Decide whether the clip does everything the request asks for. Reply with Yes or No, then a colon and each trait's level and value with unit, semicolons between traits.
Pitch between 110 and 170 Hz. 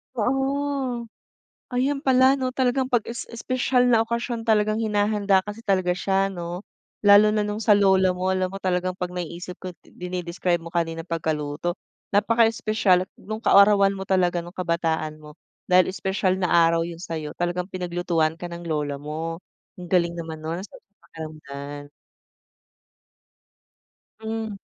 No: medium, 185 Hz